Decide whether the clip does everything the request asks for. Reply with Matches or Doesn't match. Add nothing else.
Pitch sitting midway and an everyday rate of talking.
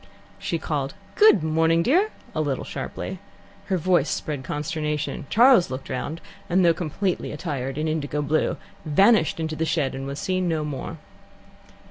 Matches